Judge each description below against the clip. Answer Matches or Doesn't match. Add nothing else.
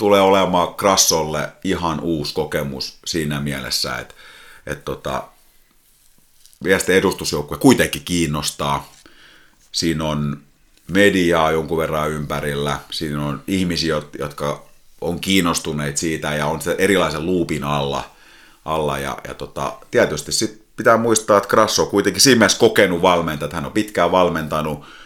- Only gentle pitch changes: Doesn't match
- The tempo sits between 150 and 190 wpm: Doesn't match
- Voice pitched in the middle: Doesn't match